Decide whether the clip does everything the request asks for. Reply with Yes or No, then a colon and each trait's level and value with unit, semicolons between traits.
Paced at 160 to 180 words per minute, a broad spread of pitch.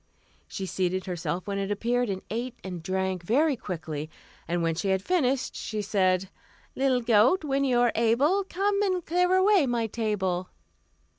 Yes: average, 165 wpm; wide, 6.5 semitones